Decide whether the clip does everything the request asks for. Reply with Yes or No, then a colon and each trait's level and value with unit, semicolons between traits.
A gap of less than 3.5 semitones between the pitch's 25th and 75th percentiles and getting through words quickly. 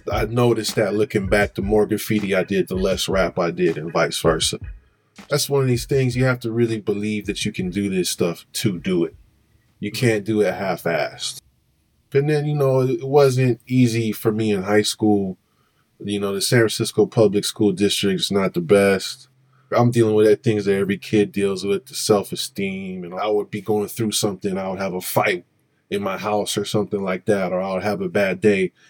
Yes: average, 2.7 semitones; fast, 220 wpm